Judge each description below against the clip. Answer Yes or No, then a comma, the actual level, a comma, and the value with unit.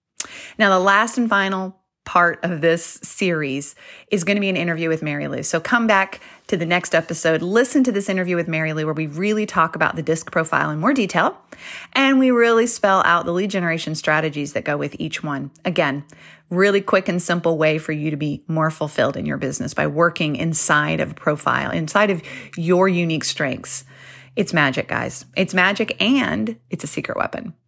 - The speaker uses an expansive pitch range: No, average, 4.0 semitones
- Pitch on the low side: No, medium, 170 Hz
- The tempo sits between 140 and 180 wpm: No, average, 200 wpm